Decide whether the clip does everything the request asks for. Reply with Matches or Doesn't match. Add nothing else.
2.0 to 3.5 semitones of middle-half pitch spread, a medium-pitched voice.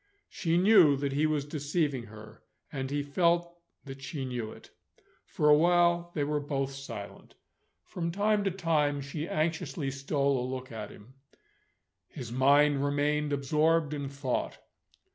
Matches